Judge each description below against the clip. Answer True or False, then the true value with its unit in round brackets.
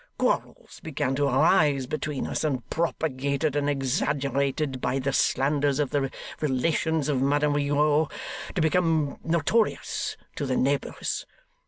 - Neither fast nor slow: False (130 wpm)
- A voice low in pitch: False (145 Hz)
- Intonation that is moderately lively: False (2.1 semitones)